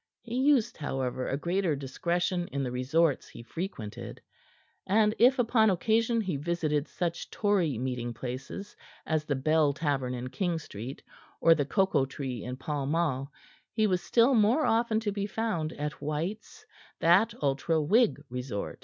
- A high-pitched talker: No, medium, 160 Hz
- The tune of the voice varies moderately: No, wide, 7.2 semitones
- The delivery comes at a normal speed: Yes, average, 155 wpm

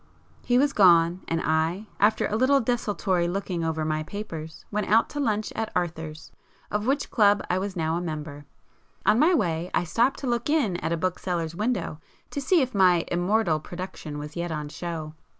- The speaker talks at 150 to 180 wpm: No, average, 190 wpm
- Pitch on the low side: No, medium, 180 Hz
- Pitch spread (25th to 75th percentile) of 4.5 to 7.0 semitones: Yes, average, 5.2 semitones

